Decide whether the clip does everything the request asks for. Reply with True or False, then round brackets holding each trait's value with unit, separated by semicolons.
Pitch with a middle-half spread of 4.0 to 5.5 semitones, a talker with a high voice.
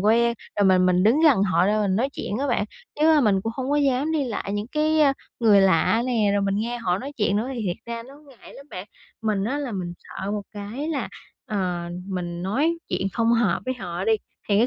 True (4.9 semitones; 215 Hz)